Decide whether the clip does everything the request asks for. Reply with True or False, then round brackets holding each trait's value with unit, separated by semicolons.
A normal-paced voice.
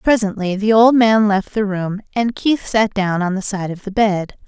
False (230 wpm)